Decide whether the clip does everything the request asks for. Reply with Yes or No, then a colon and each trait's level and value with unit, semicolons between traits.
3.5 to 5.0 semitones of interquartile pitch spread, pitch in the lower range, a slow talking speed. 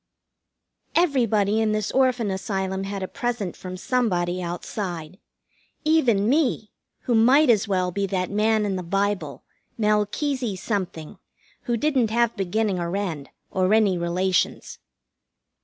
No: average, 3.8 semitones; high, 205 Hz; slow, 130 wpm